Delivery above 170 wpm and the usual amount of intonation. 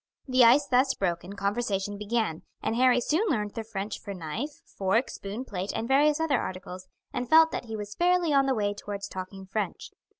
Yes: average, 195 wpm; average, 5.0 semitones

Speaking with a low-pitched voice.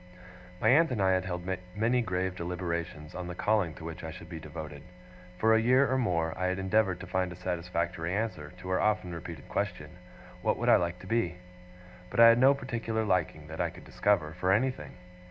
Yes: very low, 90 Hz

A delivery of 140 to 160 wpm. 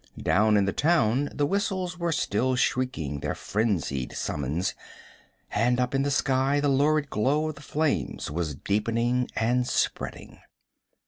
Yes: average, 145 wpm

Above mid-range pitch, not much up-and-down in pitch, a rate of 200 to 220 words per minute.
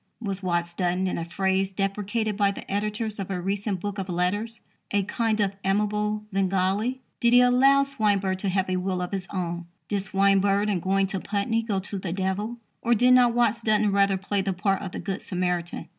Yes: high, 195 Hz; narrow, 2.1 semitones; fast, 205 wpm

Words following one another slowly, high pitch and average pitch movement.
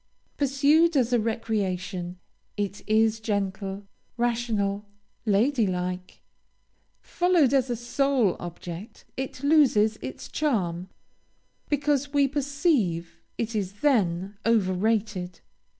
No: slow, 105 wpm; high, 220 Hz; wide, 6.1 semitones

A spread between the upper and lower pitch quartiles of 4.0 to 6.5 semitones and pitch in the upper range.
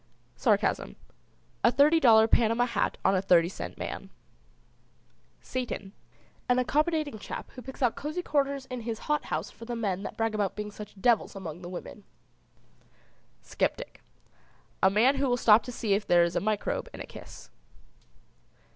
Yes: average, 4.6 semitones; high, 230 Hz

